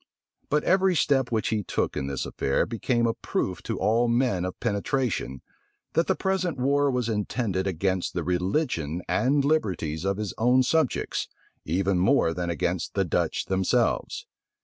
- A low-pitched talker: Yes, low, 110 Hz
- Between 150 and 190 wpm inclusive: Yes, average, 160 wpm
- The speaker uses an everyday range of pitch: No, wide, 6.5 semitones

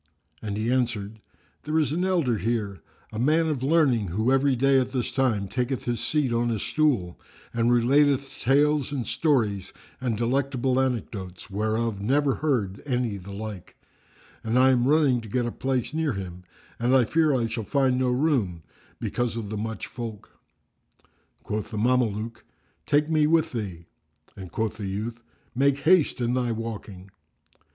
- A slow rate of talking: No, average, 165 wpm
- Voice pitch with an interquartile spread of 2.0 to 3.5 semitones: No, average, 4.0 semitones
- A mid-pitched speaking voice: No, low, 120 Hz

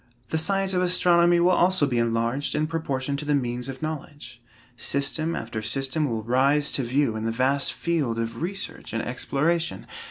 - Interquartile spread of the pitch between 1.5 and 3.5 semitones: No, average, 5.3 semitones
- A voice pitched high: No, medium, 140 Hz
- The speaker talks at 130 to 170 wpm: No, average, 180 wpm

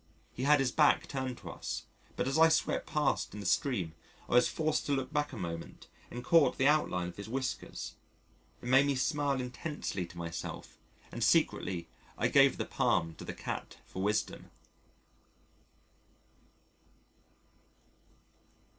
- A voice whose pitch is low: Yes, low, 130 Hz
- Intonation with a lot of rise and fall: Yes, wide, 6.7 semitones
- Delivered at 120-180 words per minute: Yes, average, 155 wpm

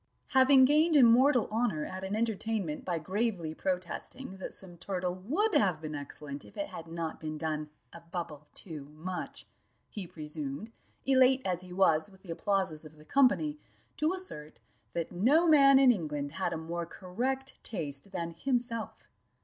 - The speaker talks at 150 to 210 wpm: Yes, average, 165 wpm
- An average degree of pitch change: No, wide, 7.6 semitones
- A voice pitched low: No, medium, 185 Hz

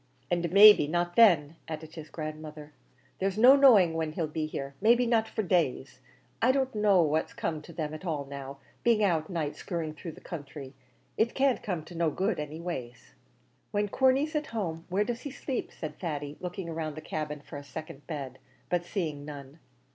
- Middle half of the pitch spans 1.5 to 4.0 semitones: No, wide, 5.4 semitones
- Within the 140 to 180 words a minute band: No, average, 195 wpm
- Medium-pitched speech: Yes, medium, 165 Hz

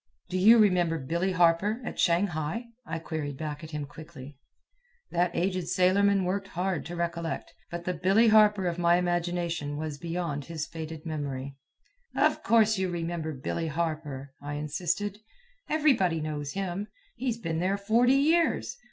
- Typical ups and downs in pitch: Yes, average, 3.7 semitones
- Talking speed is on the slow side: No, average, 150 wpm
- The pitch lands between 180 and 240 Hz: No, medium, 170 Hz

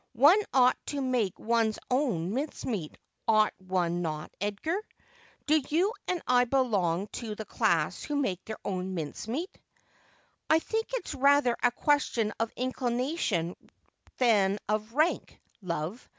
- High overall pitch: Yes, high, 235 Hz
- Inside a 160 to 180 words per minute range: No, average, 140 wpm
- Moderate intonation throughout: No, wide, 6.5 semitones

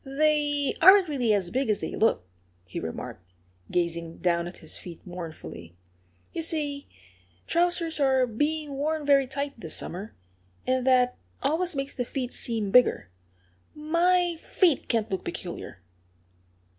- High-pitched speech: Yes, very high, 265 Hz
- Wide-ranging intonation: Yes, wide, 7.8 semitones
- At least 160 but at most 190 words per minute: No, average, 140 wpm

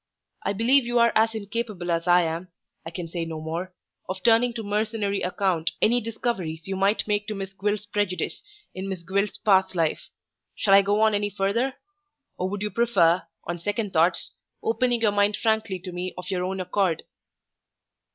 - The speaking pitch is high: Yes, high, 200 Hz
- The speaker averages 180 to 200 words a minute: Yes, average, 185 wpm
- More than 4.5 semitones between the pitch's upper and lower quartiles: No, average, 3.2 semitones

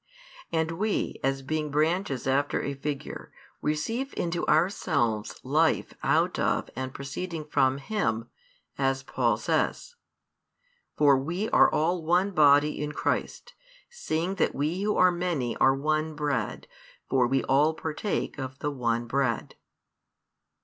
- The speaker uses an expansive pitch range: No, average, 3.8 semitones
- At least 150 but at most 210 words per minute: No, slow, 135 wpm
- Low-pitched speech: No, medium, 150 Hz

